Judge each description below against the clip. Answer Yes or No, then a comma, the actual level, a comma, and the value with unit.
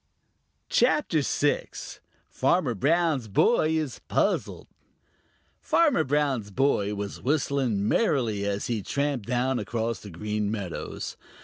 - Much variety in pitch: Yes, wide, 5.9 semitones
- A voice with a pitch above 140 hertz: No, low, 125 Hz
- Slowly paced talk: Yes, slow, 110 wpm